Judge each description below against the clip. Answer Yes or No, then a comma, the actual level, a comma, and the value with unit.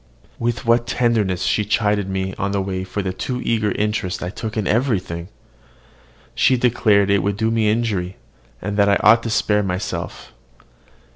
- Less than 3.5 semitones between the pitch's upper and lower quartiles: Yes, average, 2.9 semitones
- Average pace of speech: Yes, average, 170 wpm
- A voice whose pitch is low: Yes, low, 105 Hz